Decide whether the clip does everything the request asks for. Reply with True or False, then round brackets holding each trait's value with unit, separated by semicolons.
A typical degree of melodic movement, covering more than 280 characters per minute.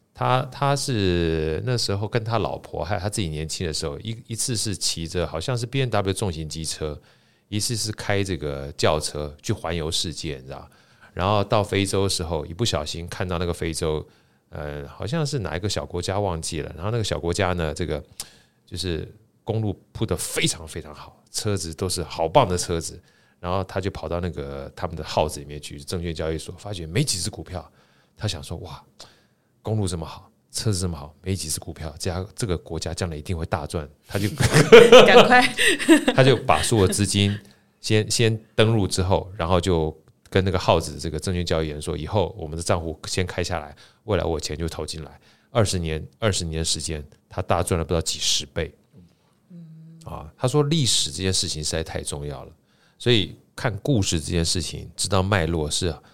True (4.9 semitones; 290 characters per minute)